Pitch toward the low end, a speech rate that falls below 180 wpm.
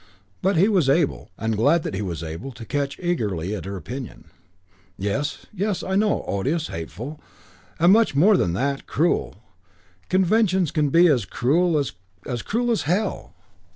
No: medium, 145 Hz; average, 160 wpm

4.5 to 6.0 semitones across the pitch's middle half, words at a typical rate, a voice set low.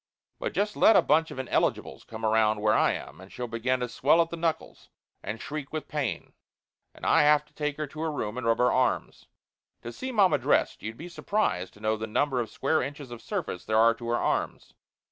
No: wide, 5.5 semitones; fast, 230 wpm; low, 130 Hz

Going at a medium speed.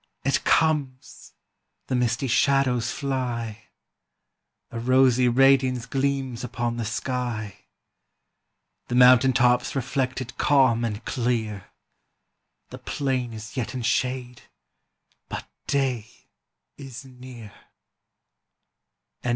No: slow, 95 wpm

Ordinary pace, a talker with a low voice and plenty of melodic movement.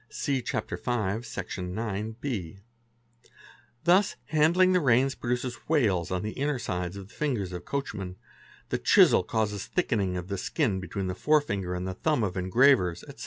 Yes: average, 160 wpm; low, 110 Hz; wide, 6.9 semitones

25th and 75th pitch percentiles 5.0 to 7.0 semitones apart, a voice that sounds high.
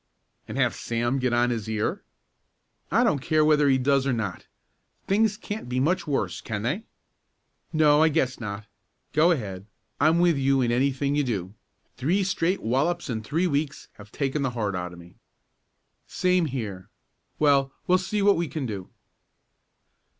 No: wide, 5.6 semitones; low, 135 Hz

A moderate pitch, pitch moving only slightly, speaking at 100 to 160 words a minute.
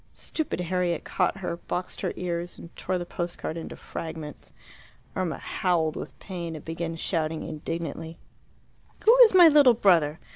Yes: medium, 170 Hz; narrow, 2.2 semitones; average, 155 wpm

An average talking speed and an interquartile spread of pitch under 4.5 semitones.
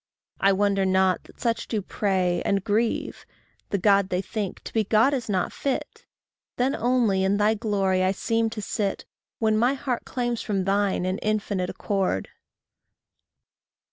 Yes: average, 160 wpm; average, 2.9 semitones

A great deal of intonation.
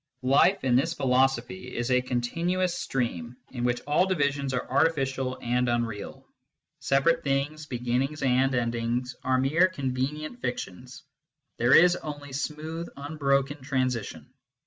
No: average, 3.3 semitones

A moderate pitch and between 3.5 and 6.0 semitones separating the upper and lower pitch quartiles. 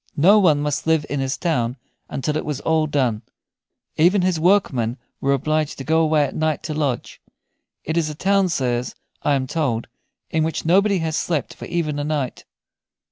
No: medium, 155 Hz; average, 2.9 semitones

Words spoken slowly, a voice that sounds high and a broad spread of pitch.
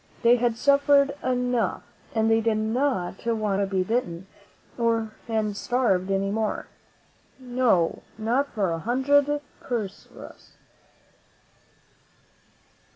No: slow, 105 wpm; high, 225 Hz; average, 3.8 semitones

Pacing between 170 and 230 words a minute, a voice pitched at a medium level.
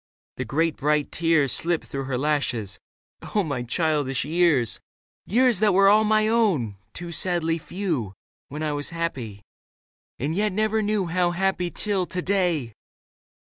No: average, 160 wpm; medium, 165 Hz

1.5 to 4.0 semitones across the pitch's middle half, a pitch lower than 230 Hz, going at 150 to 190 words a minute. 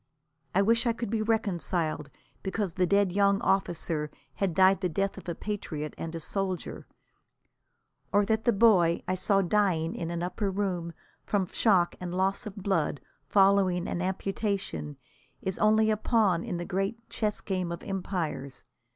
Yes: average, 2.9 semitones; high, 190 Hz; average, 165 wpm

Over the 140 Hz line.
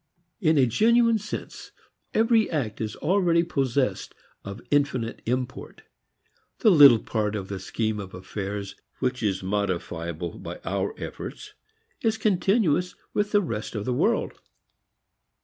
No: low, 125 Hz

